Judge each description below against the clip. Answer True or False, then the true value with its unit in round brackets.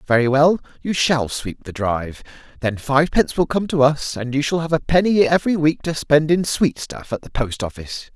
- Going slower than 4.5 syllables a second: False (5.4 syllables/s)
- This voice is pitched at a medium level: True (145 Hz)